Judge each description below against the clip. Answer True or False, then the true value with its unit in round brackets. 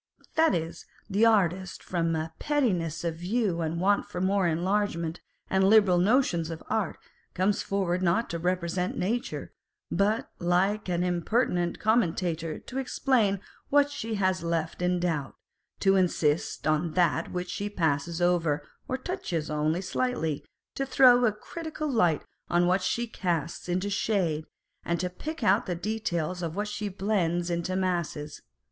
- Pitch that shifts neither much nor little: True (3.7 semitones)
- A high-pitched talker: False (180 Hz)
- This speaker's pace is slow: False (155 wpm)